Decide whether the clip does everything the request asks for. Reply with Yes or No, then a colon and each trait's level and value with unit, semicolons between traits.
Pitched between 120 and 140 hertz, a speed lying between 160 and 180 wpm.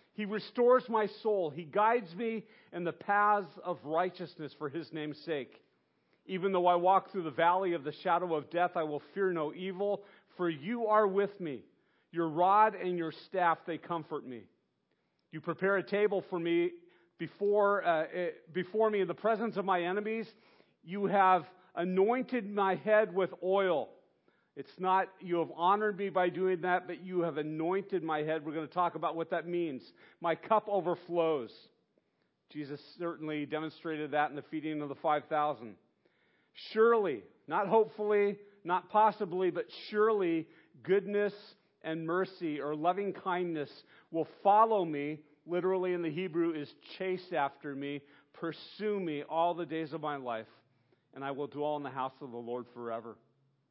No: medium, 175 Hz; average, 165 wpm